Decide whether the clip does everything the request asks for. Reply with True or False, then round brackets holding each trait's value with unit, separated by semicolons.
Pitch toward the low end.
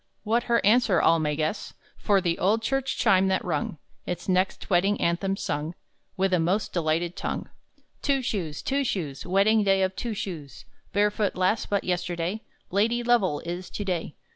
False (190 Hz)